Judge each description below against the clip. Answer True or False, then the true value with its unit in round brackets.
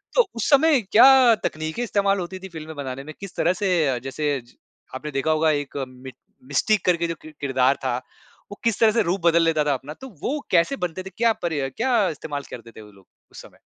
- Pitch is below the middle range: False (165 Hz)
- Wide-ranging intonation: True (6.4 semitones)